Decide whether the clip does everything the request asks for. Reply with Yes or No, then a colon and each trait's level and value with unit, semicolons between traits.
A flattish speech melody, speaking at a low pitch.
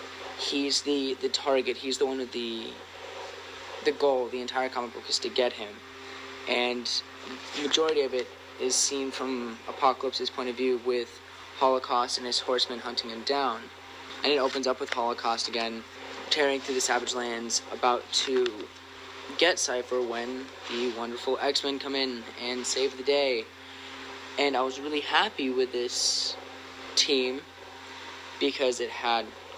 Yes: narrow, 2.1 semitones; low, 130 Hz